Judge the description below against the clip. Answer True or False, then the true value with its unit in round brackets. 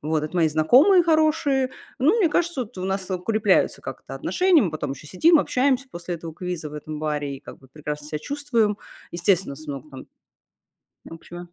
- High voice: False (180 Hz)